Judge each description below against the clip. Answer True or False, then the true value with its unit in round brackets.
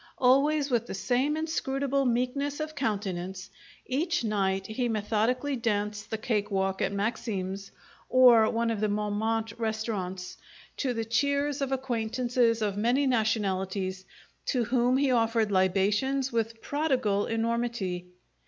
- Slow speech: True (130 wpm)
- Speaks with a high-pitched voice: True (225 Hz)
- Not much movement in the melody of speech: False (3.9 semitones)